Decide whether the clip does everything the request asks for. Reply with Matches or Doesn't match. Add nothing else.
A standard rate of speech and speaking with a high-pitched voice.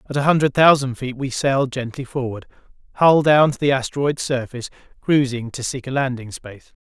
Doesn't match